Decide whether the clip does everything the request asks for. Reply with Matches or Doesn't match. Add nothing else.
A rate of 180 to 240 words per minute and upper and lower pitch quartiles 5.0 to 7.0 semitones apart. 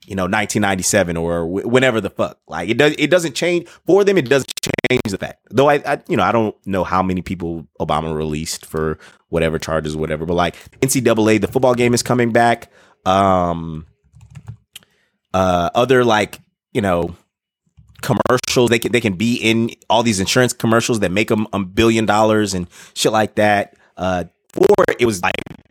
Matches